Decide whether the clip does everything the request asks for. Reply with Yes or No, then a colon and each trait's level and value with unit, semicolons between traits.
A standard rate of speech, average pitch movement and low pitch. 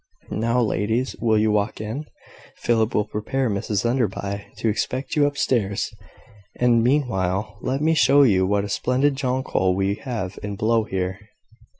Yes: average, 160 wpm; average, 4.0 semitones; low, 110 Hz